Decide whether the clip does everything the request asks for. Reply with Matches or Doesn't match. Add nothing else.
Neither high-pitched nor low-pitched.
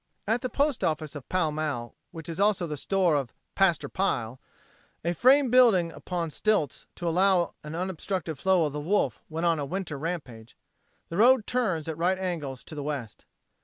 Matches